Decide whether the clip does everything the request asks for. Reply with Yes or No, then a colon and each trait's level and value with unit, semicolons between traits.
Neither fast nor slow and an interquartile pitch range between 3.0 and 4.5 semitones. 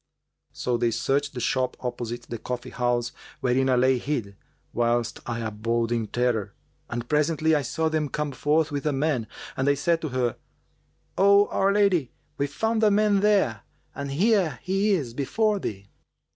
No: average, 170 wpm; average, 5.2 semitones